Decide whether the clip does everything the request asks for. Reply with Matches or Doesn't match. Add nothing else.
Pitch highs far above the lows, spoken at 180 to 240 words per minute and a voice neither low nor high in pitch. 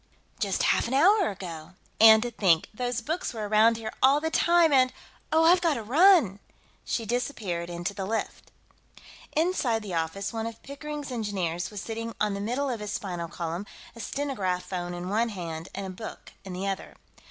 Doesn't match